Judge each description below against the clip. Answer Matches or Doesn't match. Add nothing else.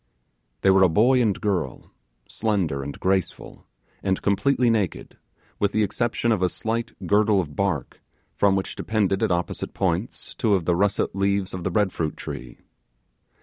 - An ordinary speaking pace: Matches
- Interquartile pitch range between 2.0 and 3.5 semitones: Matches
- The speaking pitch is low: Matches